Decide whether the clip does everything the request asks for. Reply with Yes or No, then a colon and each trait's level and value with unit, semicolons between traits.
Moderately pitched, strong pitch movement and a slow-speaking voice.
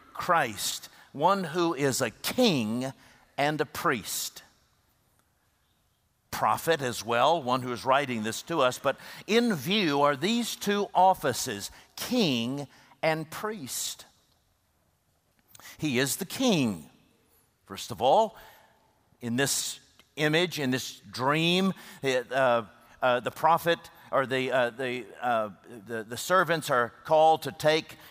Yes: medium, 145 Hz; wide, 6.1 semitones; slow, 125 wpm